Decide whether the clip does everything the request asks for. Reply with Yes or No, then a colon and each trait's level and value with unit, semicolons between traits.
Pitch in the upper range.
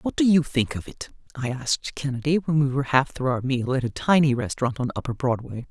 No: low, 135 Hz